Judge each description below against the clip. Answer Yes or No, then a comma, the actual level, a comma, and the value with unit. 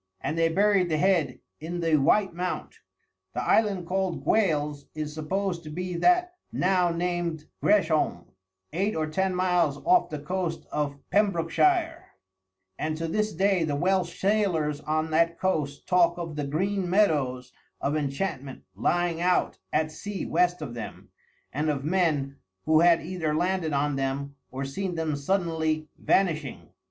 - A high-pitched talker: No, medium, 165 Hz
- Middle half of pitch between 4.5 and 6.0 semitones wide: No, average, 3.7 semitones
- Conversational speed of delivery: Yes, average, 150 wpm